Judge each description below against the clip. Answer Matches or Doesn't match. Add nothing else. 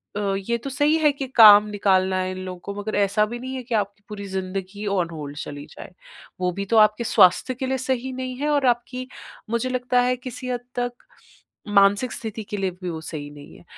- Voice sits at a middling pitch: Doesn't match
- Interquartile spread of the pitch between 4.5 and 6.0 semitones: Matches